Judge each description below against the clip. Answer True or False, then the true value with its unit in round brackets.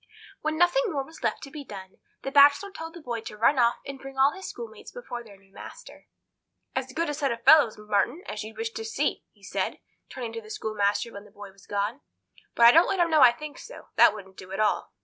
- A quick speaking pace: True (245 wpm)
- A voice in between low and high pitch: False (260 Hz)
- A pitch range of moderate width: False (6.7 semitones)